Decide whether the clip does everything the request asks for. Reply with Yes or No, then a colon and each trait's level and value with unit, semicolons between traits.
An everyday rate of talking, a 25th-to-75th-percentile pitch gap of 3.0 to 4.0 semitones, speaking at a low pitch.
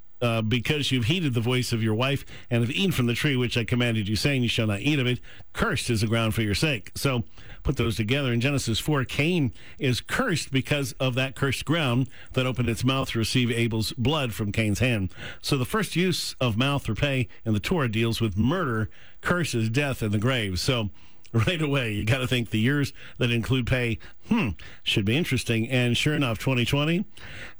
No: fast, 215 wpm; average, 3.3 semitones; low, 120 Hz